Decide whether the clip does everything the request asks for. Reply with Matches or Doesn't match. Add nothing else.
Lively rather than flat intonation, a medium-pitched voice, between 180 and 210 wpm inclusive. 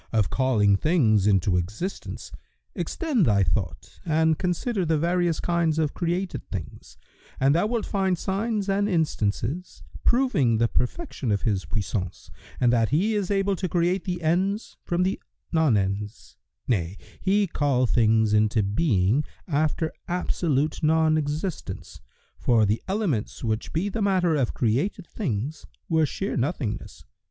Doesn't match